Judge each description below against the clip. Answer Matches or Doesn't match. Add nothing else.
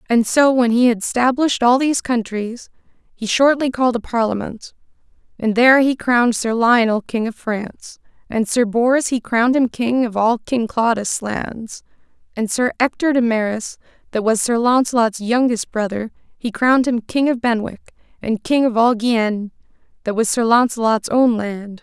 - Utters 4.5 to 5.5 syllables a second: Matches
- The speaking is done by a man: Doesn't match